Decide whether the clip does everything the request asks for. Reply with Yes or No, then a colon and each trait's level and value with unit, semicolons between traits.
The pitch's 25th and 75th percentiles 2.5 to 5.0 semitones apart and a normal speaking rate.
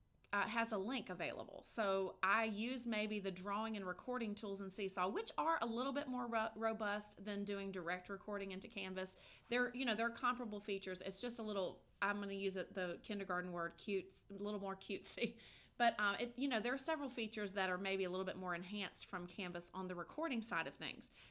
No: average, 3.3 semitones; fast, 220 wpm